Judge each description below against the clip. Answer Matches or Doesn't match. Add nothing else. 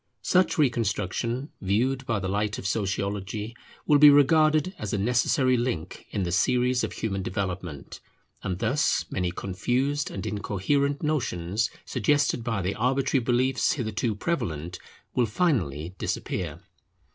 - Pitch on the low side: Matches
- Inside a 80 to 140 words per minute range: Matches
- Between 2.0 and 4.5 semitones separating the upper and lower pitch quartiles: Doesn't match